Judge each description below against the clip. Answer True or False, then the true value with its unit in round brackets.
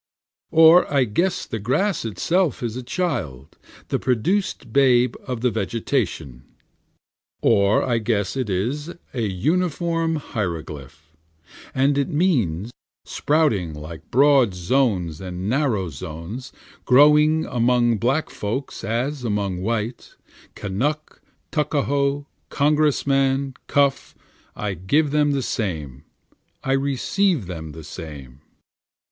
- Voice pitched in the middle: False (125 Hz)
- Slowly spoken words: True (115 wpm)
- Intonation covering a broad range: True (7.2 semitones)